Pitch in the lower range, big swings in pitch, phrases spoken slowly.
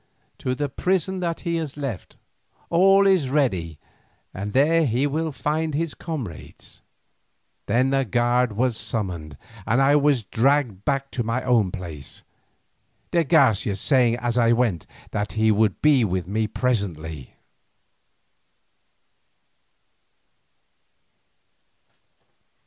Yes: low, 125 Hz; wide, 5.9 semitones; slow, 115 wpm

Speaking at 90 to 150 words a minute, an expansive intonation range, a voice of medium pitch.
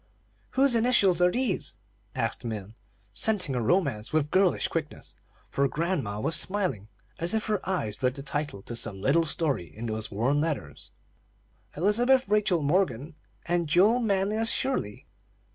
Yes: average, 145 wpm; wide, 8.6 semitones; medium, 165 Hz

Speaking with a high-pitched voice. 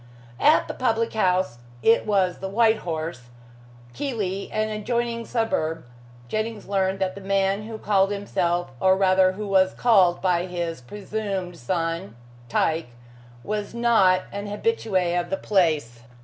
Yes: high, 195 Hz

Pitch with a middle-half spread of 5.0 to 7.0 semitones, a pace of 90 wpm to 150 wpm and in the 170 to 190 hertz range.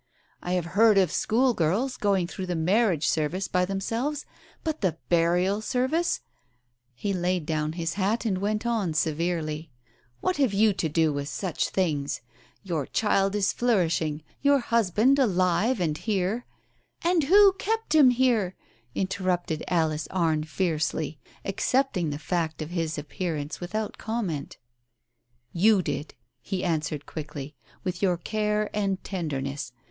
Yes: average, 5.3 semitones; average, 145 wpm; medium, 185 Hz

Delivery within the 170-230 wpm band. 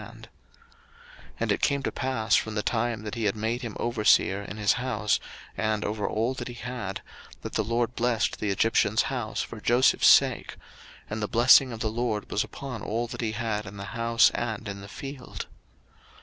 Yes: average, 195 wpm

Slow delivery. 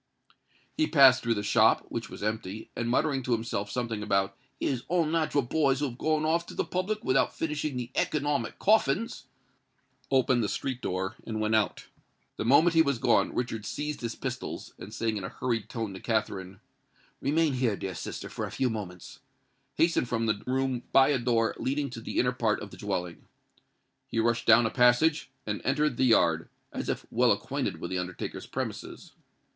No: average, 185 wpm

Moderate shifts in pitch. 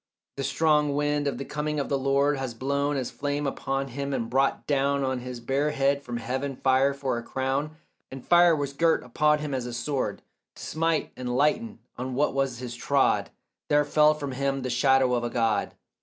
No: narrow, 2.1 semitones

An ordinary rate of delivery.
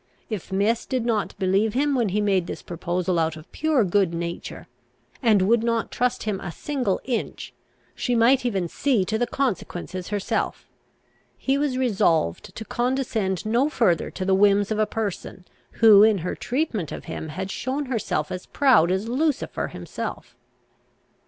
Yes: average, 165 wpm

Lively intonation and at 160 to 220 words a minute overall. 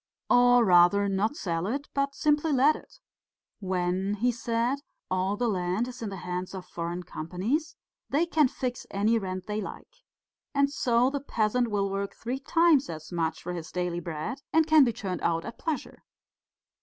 Yes: wide, 6.6 semitones; average, 180 wpm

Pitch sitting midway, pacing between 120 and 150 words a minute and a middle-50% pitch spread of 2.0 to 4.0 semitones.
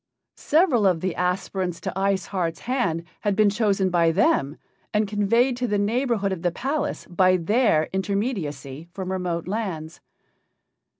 No: high, 195 Hz; average, 145 wpm; average, 3.7 semitones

